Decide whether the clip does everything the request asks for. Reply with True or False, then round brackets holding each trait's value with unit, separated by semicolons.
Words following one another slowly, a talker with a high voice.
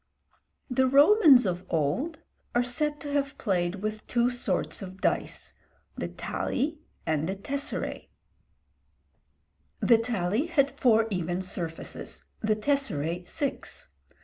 True (120 wpm; 230 Hz)